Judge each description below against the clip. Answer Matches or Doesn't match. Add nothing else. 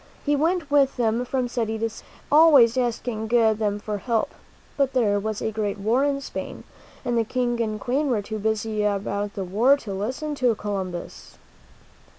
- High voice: Matches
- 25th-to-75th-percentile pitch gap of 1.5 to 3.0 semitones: Doesn't match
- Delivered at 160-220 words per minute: Matches